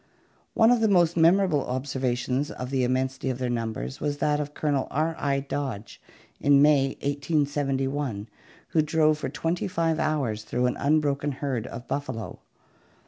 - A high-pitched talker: No, medium, 140 Hz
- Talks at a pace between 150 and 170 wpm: Yes, average, 160 wpm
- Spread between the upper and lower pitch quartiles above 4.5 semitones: No, average, 3.0 semitones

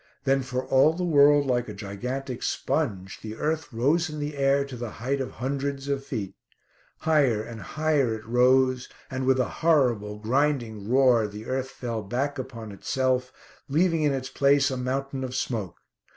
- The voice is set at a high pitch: No, low, 130 Hz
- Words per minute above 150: Yes, average, 175 wpm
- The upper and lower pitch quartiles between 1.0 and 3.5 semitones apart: Yes, average, 3.2 semitones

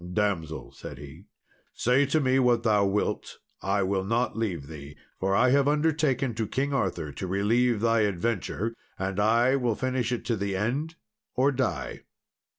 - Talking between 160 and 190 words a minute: Yes, average, 165 wpm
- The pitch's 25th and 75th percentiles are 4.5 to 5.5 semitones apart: Yes, average, 4.9 semitones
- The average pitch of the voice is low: Yes, low, 115 Hz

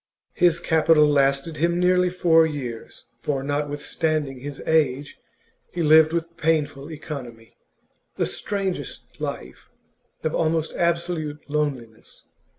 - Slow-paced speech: Yes, slow, 110 wpm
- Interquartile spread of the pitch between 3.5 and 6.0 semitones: No, narrow, 2.6 semitones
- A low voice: No, medium, 155 Hz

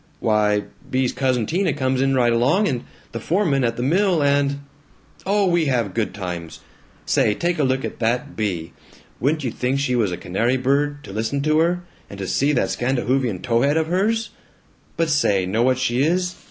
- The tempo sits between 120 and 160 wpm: No, average, 195 wpm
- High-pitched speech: No, low, 130 Hz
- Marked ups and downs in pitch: No, average, 4.8 semitones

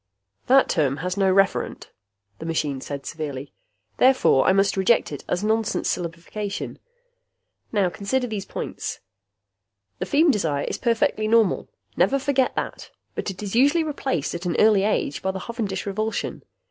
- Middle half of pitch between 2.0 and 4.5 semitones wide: No, average, 5.1 semitones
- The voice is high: Yes, high, 200 Hz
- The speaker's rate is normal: Yes, average, 155 wpm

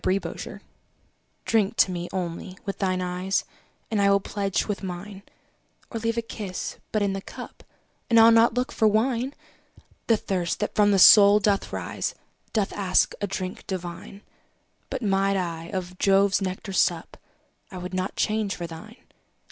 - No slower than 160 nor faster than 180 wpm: Yes, average, 175 wpm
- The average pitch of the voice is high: Yes, high, 195 Hz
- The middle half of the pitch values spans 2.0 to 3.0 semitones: Yes, narrow, 2.6 semitones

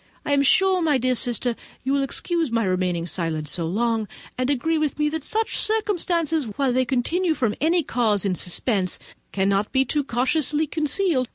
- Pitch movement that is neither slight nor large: No, wide, 6.4 semitones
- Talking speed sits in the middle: Yes, average, 180 wpm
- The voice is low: No, very high, 265 Hz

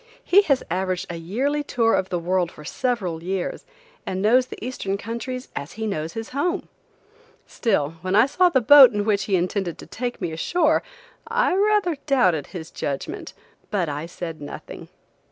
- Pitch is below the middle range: No, high, 205 Hz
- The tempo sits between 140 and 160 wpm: No, average, 175 wpm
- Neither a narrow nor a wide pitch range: No, wide, 6.9 semitones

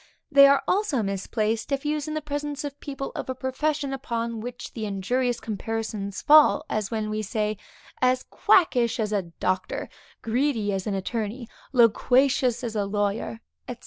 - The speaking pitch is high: Yes, high, 235 Hz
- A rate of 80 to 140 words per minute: No, average, 165 wpm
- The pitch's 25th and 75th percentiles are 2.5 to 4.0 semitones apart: No, average, 4.5 semitones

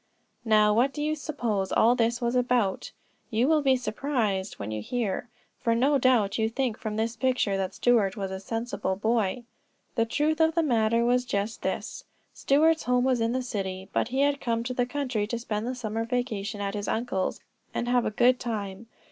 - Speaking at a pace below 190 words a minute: No, average, 200 wpm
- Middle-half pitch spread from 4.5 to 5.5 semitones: No, average, 3.2 semitones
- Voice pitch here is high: Yes, high, 235 Hz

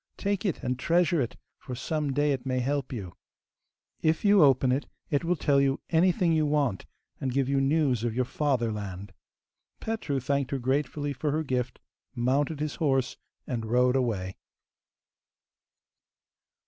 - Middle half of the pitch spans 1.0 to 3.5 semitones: Yes, average, 3.2 semitones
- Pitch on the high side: No, low, 135 Hz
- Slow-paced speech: No, average, 155 wpm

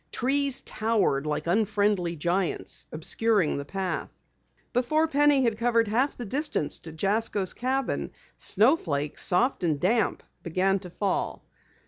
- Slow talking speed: Yes, slow, 125 wpm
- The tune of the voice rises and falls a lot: Yes, wide, 5.7 semitones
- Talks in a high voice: Yes, high, 210 Hz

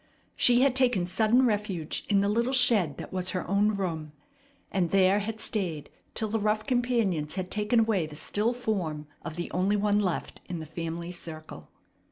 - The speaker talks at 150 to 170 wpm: No, average, 185 wpm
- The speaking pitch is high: Yes, high, 200 Hz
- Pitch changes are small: No, average, 4.4 semitones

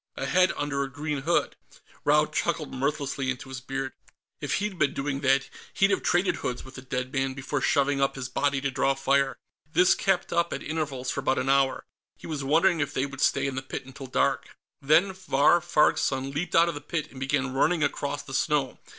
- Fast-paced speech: Yes, fast, 220 wpm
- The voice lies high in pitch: No, medium, 140 Hz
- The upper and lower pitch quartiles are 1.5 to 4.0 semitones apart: Yes, narrow, 2.4 semitones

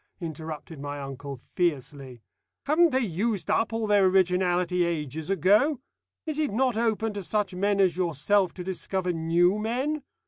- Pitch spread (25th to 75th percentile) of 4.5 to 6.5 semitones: Yes, average, 5.0 semitones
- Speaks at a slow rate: No, average, 150 wpm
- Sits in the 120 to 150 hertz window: No, medium, 185 Hz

